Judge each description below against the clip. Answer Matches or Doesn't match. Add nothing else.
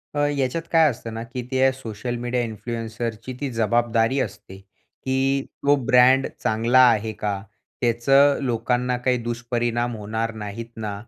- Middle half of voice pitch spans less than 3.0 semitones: Matches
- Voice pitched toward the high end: Doesn't match